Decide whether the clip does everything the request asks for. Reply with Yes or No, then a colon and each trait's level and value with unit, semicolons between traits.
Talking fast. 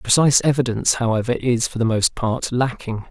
No: average, 175 wpm